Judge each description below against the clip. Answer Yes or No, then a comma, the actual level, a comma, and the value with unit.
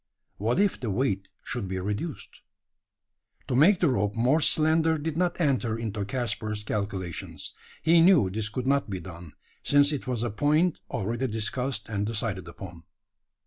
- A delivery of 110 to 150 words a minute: No, average, 160 wpm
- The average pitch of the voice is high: No, low, 115 Hz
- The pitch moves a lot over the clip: Yes, wide, 6.3 semitones